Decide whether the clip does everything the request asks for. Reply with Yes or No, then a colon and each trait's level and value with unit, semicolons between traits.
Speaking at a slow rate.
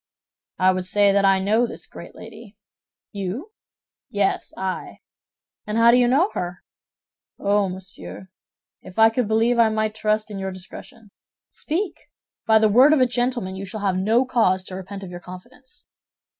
No: average, 170 wpm